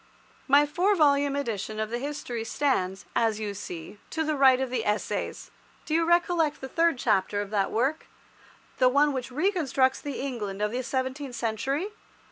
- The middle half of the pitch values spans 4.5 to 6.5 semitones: Yes, average, 5.0 semitones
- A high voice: Yes, very high, 260 Hz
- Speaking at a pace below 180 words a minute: Yes, average, 170 wpm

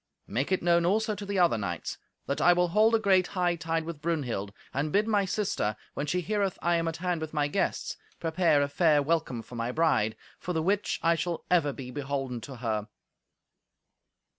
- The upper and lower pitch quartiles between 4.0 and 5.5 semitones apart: Yes, average, 4.5 semitones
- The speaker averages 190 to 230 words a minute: Yes, average, 200 wpm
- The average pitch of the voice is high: No, medium, 165 Hz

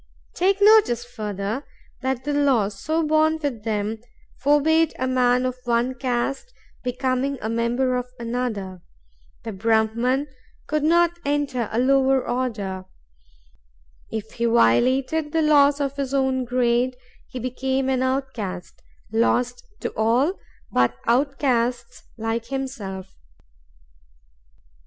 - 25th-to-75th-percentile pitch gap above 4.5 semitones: No, average, 3.2 semitones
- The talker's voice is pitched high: Yes, very high, 255 Hz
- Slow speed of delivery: Yes, slow, 120 wpm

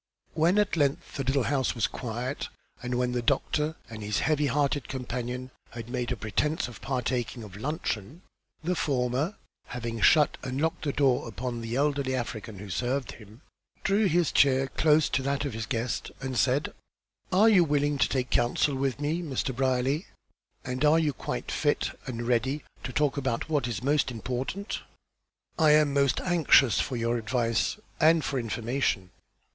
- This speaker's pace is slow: No, average, 175 wpm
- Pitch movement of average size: Yes, average, 3.6 semitones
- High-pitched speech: No, low, 130 Hz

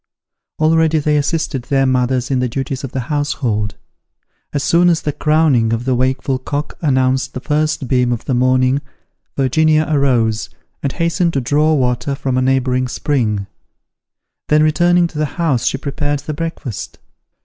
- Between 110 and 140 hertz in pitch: Yes, low, 135 Hz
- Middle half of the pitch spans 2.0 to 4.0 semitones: Yes, average, 3.1 semitones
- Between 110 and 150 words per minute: No, average, 160 wpm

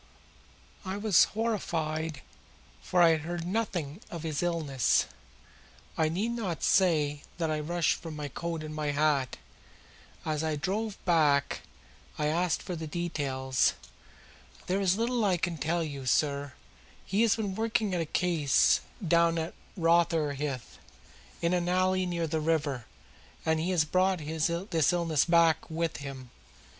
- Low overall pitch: No, medium, 165 Hz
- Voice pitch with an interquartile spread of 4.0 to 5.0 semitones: No, average, 3.0 semitones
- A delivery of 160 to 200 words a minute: No, average, 150 wpm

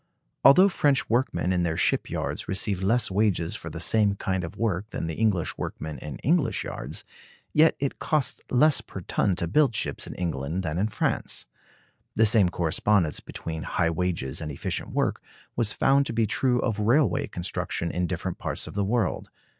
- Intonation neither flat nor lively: No, wide, 5.8 semitones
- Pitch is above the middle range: No, low, 100 Hz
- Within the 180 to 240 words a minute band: Yes, average, 185 wpm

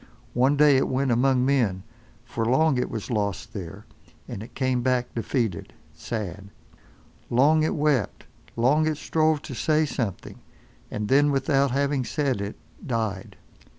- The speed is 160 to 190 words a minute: No, average, 145 wpm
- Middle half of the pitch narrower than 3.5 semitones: No, average, 4.3 semitones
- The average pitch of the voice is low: Yes, low, 130 Hz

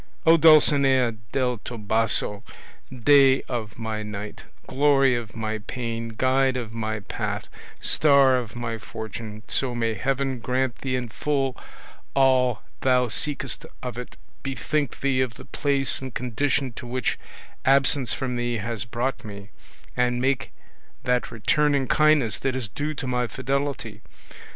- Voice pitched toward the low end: Yes, low, 125 Hz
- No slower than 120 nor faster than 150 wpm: Yes, average, 145 wpm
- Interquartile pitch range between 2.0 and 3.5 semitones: Yes, average, 3.0 semitones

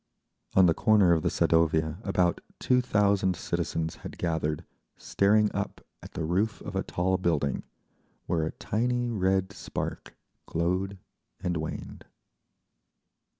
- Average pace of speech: No, slow, 130 wpm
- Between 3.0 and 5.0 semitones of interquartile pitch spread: Yes, average, 3.6 semitones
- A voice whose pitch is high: No, very low, 95 Hz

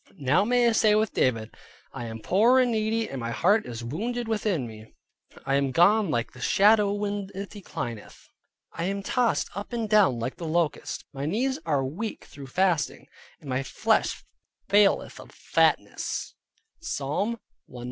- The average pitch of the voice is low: No, high, 195 Hz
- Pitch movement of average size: No, wide, 8.1 semitones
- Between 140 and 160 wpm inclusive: No, average, 170 wpm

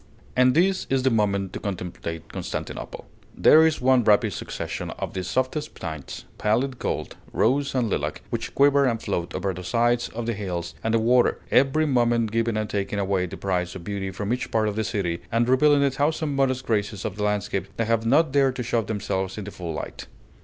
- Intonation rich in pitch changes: No, average, 4.8 semitones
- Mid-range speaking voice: No, low, 115 Hz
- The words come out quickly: Yes, fast, 210 wpm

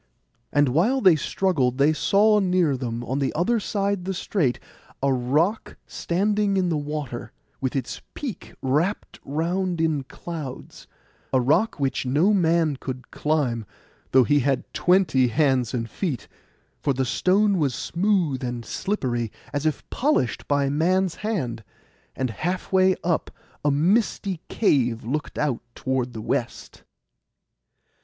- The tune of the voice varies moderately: No, wide, 6.1 semitones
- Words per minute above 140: No, slow, 135 wpm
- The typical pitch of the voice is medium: Yes, medium, 150 Hz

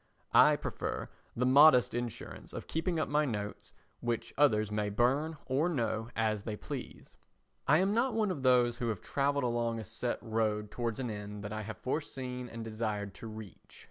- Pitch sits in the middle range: No, low, 120 Hz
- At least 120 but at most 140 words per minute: No, average, 185 wpm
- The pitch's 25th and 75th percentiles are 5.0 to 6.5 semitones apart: No, average, 4.3 semitones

